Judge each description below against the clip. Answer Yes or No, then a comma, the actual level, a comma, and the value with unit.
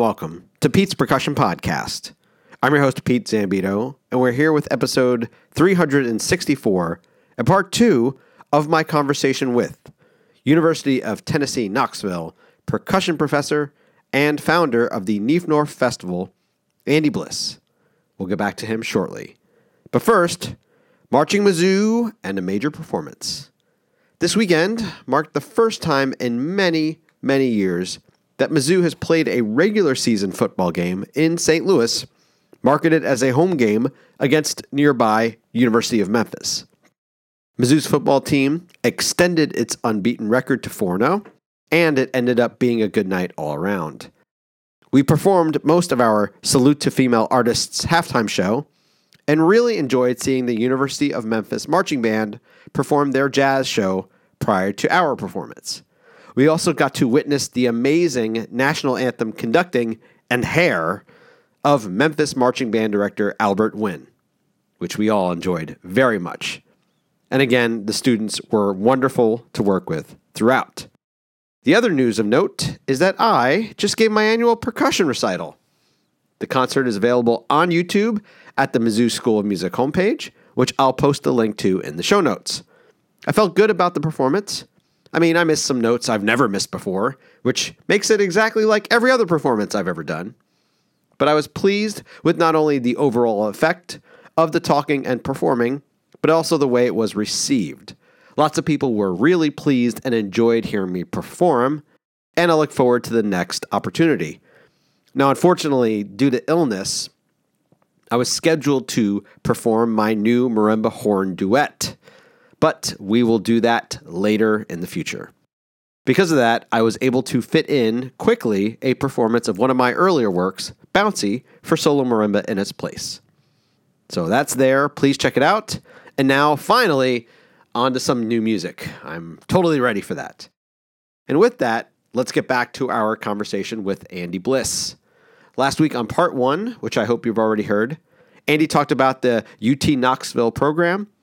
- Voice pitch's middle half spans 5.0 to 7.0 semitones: Yes, wide, 5.4 semitones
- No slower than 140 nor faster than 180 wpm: Yes, average, 160 wpm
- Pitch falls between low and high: No, low, 130 Hz